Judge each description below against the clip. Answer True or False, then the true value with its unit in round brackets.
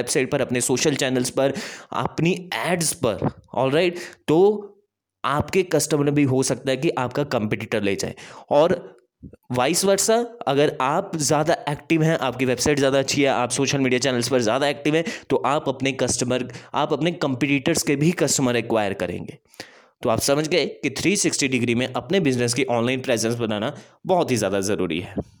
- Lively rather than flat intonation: False (4.3 semitones)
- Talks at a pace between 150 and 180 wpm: True (175 wpm)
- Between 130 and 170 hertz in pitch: True (140 Hz)